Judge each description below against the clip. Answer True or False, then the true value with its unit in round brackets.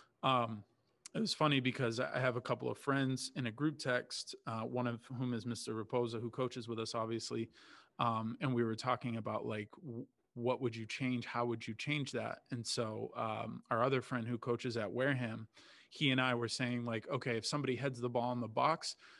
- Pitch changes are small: True (1.8 semitones)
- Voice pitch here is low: True (120 Hz)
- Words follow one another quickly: True (215 wpm)